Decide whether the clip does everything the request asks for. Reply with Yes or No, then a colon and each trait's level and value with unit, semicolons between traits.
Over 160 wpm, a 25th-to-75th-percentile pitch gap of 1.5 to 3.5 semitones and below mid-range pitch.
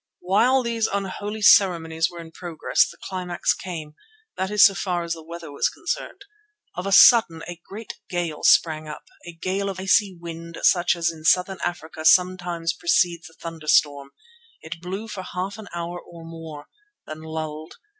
No: average, 170 wpm; average, 2.9 semitones; medium, 175 Hz